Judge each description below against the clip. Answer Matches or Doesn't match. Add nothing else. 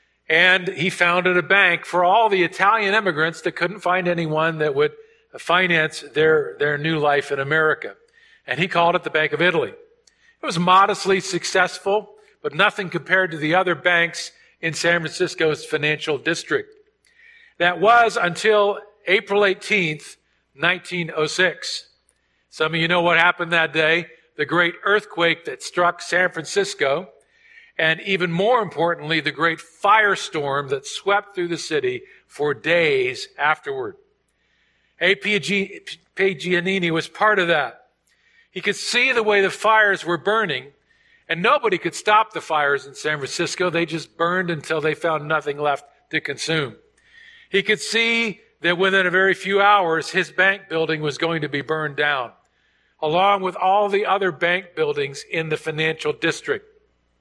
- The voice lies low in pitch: Doesn't match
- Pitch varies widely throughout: Doesn't match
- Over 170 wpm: Doesn't match